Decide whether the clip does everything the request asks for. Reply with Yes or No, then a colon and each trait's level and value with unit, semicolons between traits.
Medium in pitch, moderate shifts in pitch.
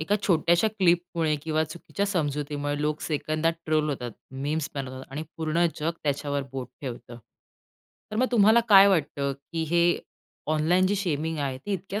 Yes: medium, 155 Hz; average, 3.5 semitones